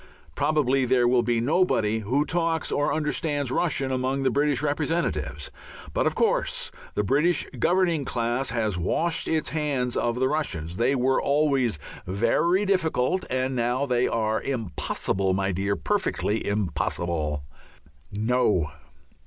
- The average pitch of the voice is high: No, low, 130 Hz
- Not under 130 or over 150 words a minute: Yes, slow, 135 wpm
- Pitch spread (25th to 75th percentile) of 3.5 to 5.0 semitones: No, wide, 5.4 semitones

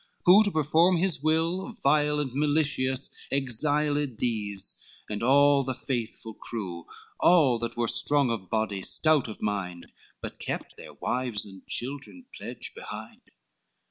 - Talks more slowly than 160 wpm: Yes, average, 140 wpm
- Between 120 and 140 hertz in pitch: Yes, low, 135 Hz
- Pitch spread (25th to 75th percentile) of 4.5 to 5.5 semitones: Yes, average, 5.2 semitones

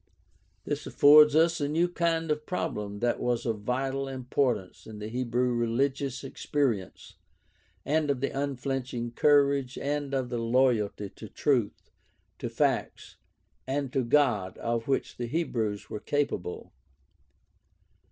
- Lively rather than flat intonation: No, average, 3.5 semitones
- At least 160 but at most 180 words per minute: No, average, 140 wpm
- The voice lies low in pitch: Yes, low, 130 Hz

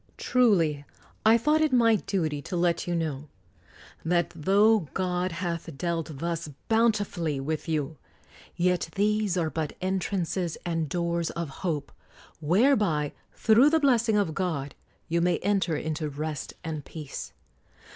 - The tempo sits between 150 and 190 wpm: No, slow, 135 wpm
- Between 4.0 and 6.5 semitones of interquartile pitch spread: Yes, average, 4.4 semitones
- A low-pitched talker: No, medium, 170 Hz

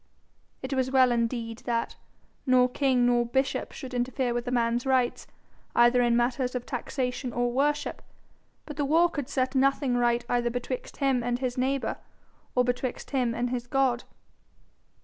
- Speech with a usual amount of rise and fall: No, narrow, 1.7 semitones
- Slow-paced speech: No, average, 165 wpm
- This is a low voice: No, very high, 250 Hz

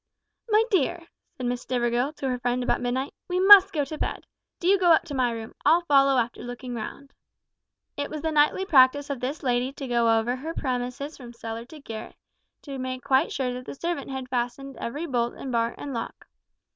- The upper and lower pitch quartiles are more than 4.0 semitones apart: No, average, 3.3 semitones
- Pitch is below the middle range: No, very high, 260 Hz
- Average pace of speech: No, fast, 210 wpm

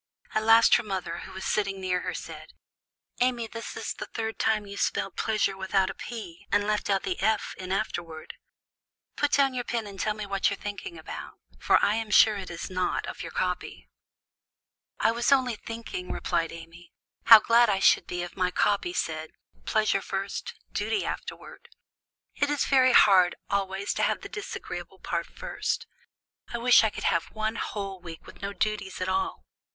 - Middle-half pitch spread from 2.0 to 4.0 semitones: Yes, average, 3.4 semitones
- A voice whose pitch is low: No, high, 200 Hz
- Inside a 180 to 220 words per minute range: Yes, average, 190 wpm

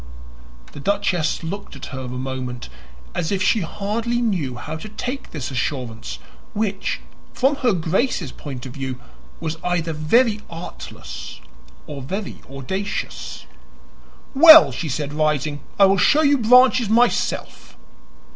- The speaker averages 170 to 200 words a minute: No, slow, 135 wpm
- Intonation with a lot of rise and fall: Yes, wide, 7.8 semitones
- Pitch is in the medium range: Yes, medium, 175 Hz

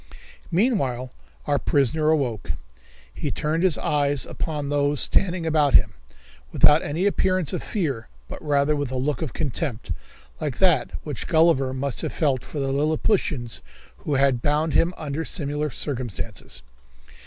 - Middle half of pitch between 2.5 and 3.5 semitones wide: Yes, average, 2.9 semitones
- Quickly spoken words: No, average, 145 wpm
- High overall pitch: No, medium, 145 Hz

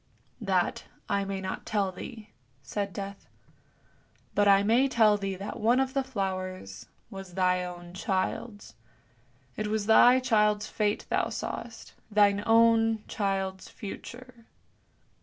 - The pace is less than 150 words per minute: Yes, slow, 135 wpm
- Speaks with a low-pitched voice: No, high, 205 Hz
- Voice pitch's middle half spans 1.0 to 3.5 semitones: Yes, average, 2.8 semitones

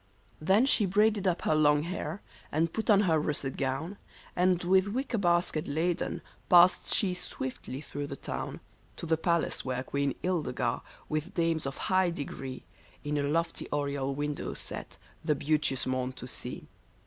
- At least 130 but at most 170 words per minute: Yes, average, 165 wpm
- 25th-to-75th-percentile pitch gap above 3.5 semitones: Yes, average, 4.2 semitones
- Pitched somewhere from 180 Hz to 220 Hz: No, medium, 160 Hz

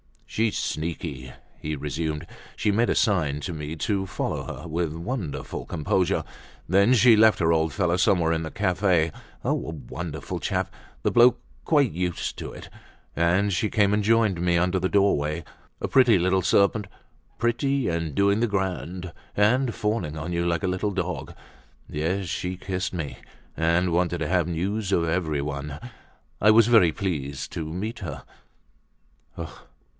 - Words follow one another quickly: No, average, 155 wpm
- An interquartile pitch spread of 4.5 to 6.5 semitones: No, average, 4.1 semitones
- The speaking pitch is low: Yes, very low, 90 Hz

